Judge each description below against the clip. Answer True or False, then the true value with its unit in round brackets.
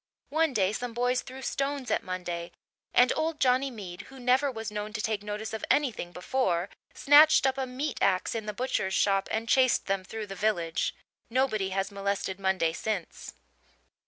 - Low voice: False (220 Hz)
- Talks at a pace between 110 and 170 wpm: False (180 wpm)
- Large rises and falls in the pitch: False (5.0 semitones)